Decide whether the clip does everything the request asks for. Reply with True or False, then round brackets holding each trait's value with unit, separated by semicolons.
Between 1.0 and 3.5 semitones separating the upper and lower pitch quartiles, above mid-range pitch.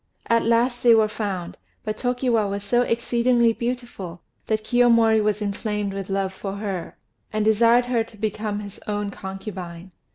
True (2.7 semitones; 215 Hz)